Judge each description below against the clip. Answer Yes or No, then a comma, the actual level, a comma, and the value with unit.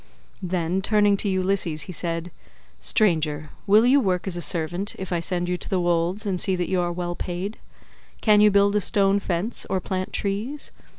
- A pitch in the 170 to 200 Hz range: Yes, medium, 185 Hz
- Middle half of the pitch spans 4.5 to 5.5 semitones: No, narrow, 2.6 semitones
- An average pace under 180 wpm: No, average, 195 wpm